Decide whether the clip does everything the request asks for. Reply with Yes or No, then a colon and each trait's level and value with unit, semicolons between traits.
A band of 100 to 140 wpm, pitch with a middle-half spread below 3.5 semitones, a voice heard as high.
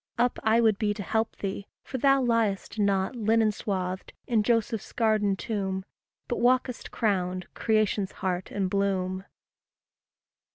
Yes: slow, 135 wpm; average, 2.9 semitones; high, 210 Hz